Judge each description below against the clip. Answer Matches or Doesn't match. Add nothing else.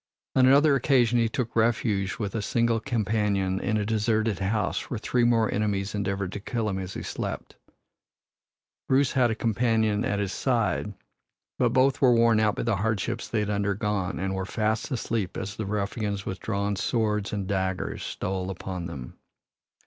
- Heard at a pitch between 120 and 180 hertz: Doesn't match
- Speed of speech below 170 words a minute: Doesn't match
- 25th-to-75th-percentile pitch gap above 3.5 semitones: Doesn't match